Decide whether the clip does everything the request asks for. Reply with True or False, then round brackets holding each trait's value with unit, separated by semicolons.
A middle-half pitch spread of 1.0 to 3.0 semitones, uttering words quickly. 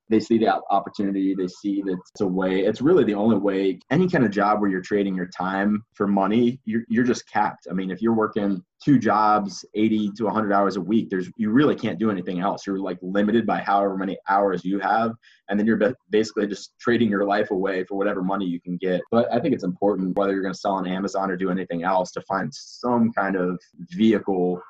True (2.4 semitones; 235 wpm)